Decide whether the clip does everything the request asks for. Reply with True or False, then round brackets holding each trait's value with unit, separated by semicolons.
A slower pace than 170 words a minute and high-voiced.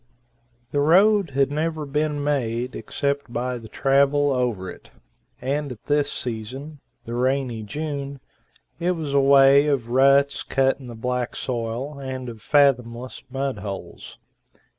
False (140 wpm; 135 Hz)